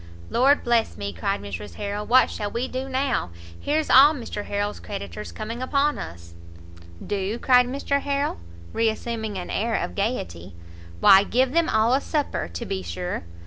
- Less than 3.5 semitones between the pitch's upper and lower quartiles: No, average, 5.1 semitones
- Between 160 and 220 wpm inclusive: Yes, average, 170 wpm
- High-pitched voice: Yes, high, 225 Hz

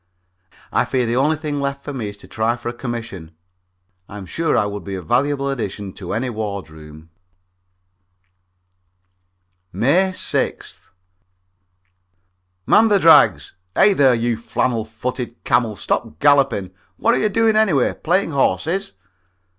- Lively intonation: Yes, wide, 5.9 semitones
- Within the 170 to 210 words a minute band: No, average, 140 wpm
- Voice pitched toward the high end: No, low, 120 Hz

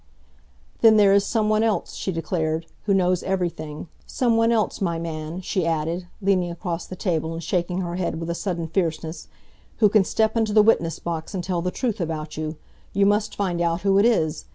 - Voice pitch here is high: No, medium, 180 Hz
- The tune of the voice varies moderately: Yes, average, 3.6 semitones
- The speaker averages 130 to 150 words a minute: No, fast, 205 wpm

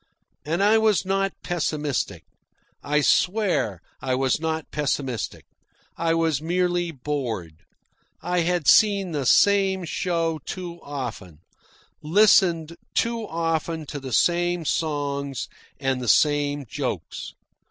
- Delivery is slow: Yes, slow, 115 wpm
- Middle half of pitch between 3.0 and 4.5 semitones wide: Yes, average, 4.0 semitones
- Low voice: No, medium, 160 Hz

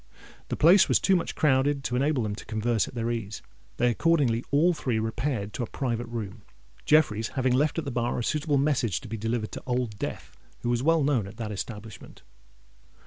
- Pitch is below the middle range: Yes, low, 120 Hz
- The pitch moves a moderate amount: Yes, average, 4.3 semitones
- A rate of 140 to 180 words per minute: No, fast, 205 wpm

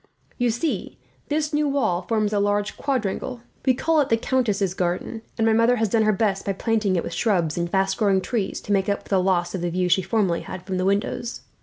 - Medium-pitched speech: No, high, 205 Hz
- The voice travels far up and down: No, average, 3.5 semitones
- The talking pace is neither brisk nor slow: No, fast, 235 wpm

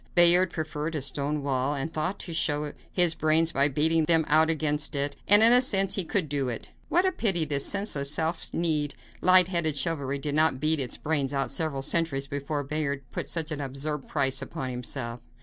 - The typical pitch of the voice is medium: Yes, medium, 155 Hz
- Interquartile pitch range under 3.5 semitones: Yes, average, 2.9 semitones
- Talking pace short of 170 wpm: No, average, 200 wpm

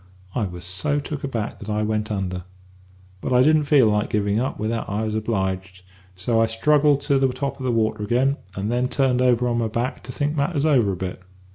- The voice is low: Yes, low, 115 Hz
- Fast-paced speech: Yes, fast, 225 wpm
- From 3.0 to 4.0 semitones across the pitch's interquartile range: No, average, 4.4 semitones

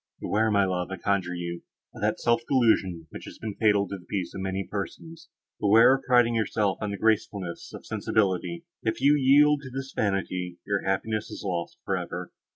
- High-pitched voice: No, low, 105 Hz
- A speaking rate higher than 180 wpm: Yes, average, 200 wpm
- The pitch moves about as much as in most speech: Yes, average, 3.8 semitones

